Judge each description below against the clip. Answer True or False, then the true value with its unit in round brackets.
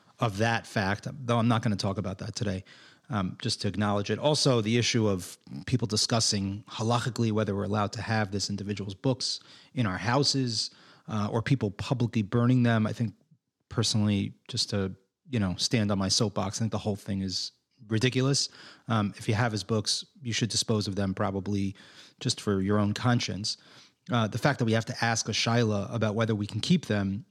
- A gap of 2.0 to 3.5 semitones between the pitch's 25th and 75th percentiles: True (2.8 semitones)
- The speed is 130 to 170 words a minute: False (200 wpm)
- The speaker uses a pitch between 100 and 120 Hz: True (110 Hz)